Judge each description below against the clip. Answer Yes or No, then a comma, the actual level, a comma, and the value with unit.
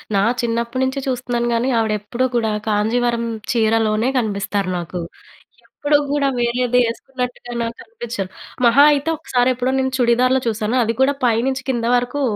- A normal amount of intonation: No, narrow, 2.3 semitones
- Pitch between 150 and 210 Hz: No, high, 240 Hz